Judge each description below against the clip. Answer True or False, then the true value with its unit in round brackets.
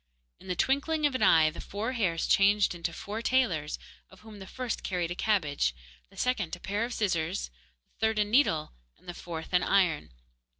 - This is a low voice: False (195 Hz)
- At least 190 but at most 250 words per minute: True (200 wpm)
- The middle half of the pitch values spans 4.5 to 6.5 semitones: True (4.8 semitones)